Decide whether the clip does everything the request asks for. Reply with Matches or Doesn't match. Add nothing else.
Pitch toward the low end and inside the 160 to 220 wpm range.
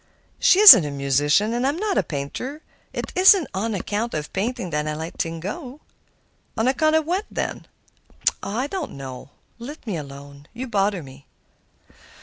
Doesn't match